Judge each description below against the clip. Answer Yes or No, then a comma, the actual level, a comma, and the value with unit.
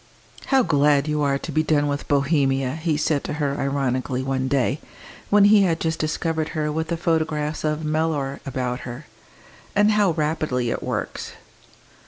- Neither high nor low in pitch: Yes, medium, 150 Hz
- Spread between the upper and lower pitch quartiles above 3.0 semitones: No, narrow, 2.6 semitones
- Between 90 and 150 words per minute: No, average, 170 wpm